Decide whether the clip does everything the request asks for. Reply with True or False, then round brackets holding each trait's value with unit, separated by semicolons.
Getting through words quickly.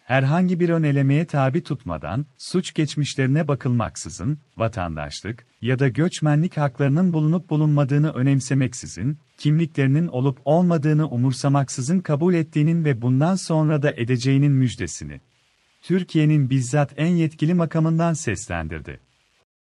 False (105 wpm)